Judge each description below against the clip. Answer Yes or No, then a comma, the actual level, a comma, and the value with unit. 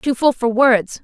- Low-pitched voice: No, high, 245 Hz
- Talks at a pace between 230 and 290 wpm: Yes, fast, 235 wpm